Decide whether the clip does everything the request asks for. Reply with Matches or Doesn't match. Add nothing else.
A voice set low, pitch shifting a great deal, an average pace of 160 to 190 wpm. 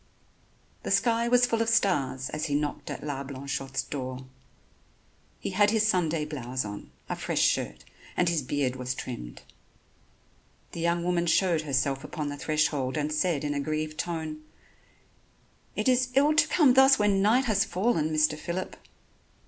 Doesn't match